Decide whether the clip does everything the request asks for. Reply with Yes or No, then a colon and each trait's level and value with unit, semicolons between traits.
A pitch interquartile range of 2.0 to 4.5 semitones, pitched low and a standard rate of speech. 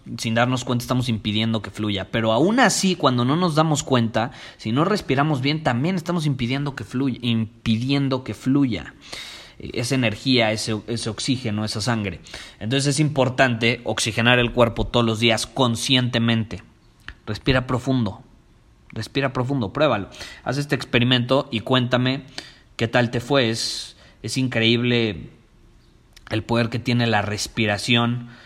Yes: average, 2.9 semitones; low, 120 Hz; average, 140 wpm